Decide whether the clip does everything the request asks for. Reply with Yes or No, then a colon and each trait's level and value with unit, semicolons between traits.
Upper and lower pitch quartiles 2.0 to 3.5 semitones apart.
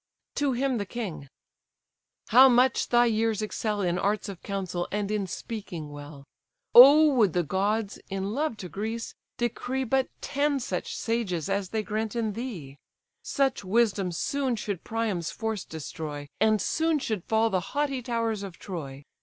No: average, 4.4 semitones